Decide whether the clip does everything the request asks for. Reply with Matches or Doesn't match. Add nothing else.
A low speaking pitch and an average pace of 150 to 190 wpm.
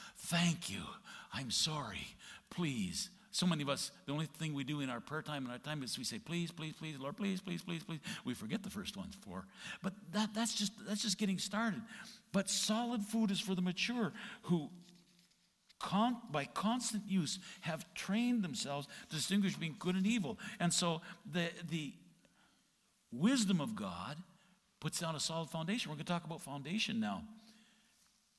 Doesn't match